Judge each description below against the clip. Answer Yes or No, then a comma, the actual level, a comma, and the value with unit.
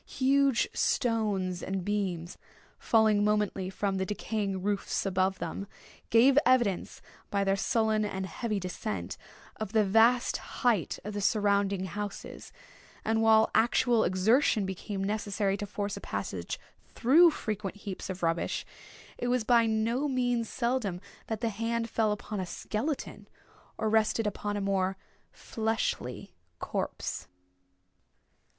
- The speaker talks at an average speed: No, slow, 130 wpm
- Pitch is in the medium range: No, high, 210 Hz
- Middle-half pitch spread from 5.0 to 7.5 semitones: No, average, 2.9 semitones